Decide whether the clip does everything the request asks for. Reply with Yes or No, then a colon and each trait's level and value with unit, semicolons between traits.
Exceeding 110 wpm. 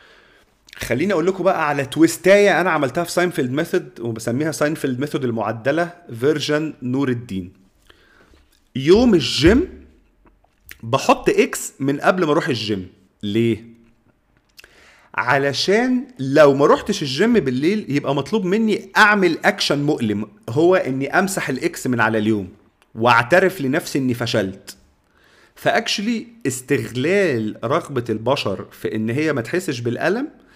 Yes: average, 120 wpm